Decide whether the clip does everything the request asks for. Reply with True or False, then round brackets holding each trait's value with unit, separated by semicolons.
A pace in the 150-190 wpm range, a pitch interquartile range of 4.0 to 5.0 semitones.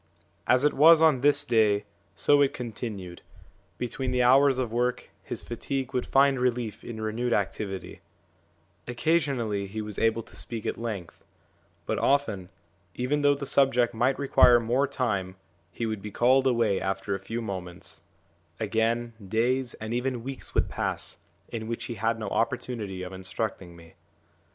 False (160 wpm; 3.6 semitones)